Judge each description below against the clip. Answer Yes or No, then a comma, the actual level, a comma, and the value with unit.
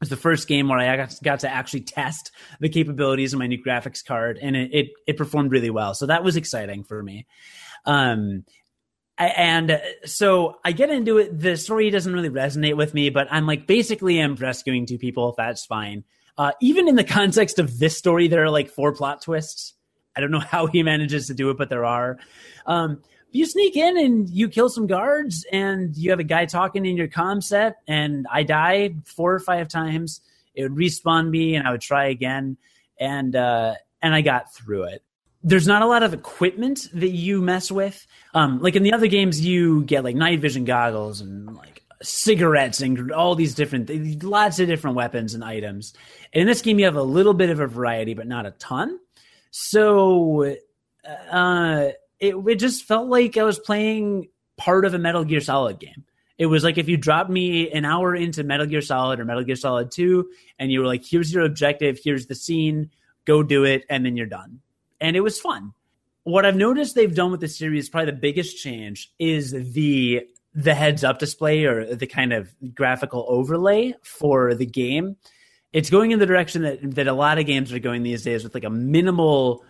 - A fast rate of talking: Yes, fast, 210 wpm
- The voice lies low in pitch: No, medium, 155 Hz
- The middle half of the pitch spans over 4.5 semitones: Yes, wide, 5.5 semitones